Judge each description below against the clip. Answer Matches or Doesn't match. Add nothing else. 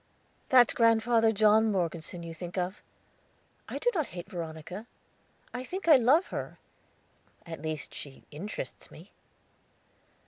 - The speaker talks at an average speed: Doesn't match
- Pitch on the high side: Matches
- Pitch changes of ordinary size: Doesn't match